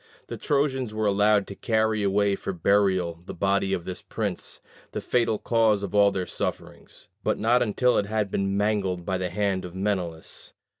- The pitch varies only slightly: Yes, narrow, 2.3 semitones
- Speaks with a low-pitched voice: Yes, low, 100 Hz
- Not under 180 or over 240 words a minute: Yes, average, 185 wpm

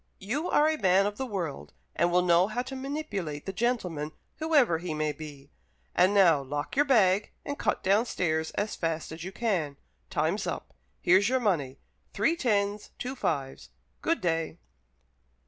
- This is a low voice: No, high, 190 Hz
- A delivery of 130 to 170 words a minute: Yes, average, 165 wpm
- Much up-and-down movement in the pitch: Yes, wide, 7.0 semitones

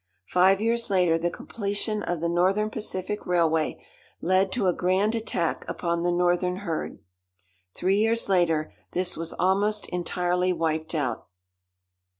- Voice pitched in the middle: Yes, medium, 180 Hz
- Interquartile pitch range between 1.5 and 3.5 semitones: Yes, average, 2.8 semitones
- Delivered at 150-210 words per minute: No, average, 140 wpm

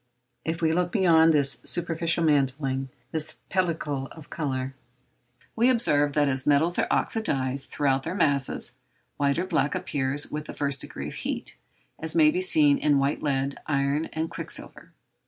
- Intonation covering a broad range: No, average, 3.3 semitones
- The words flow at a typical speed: Yes, average, 160 wpm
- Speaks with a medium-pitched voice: Yes, medium, 150 Hz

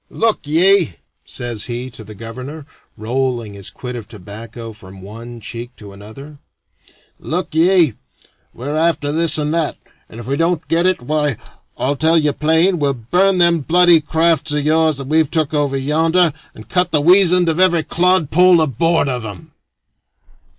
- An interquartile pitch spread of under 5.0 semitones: No, wide, 5.6 semitones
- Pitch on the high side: No, medium, 150 Hz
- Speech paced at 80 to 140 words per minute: No, average, 165 wpm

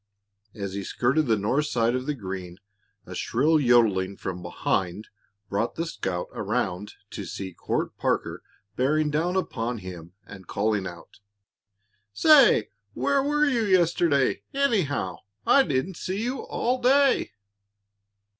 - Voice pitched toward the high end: No, low, 125 Hz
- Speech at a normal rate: No, slow, 130 wpm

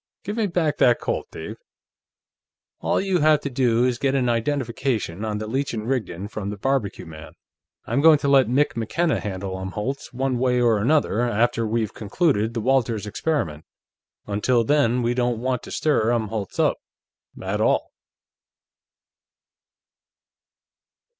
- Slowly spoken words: No, average, 150 wpm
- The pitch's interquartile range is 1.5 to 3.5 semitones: No, average, 4.2 semitones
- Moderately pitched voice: No, low, 120 Hz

